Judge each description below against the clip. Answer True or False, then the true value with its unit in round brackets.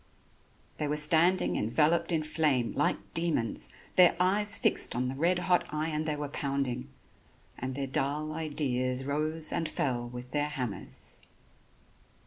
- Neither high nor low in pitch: True (150 Hz)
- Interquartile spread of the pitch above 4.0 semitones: False (3.6 semitones)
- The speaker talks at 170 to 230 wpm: False (140 wpm)